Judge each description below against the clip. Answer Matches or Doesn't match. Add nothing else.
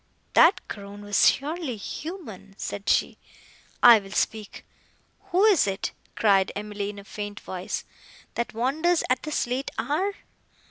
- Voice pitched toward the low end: Doesn't match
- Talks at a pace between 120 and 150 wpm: Matches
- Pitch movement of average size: Doesn't match